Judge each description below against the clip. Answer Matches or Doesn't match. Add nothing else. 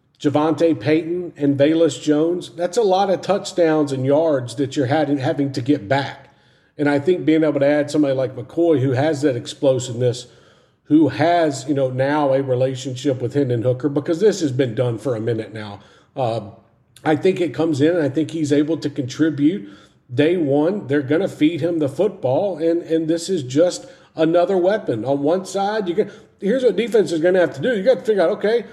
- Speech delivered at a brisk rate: Matches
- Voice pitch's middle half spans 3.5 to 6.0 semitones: Matches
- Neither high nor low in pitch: Matches